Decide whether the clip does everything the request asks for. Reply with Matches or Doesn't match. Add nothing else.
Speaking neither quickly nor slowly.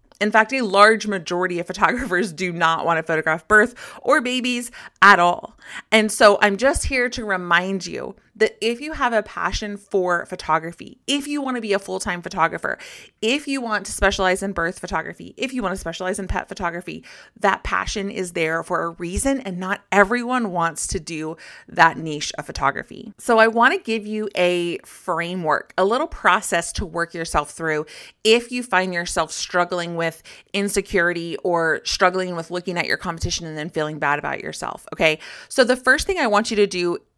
Matches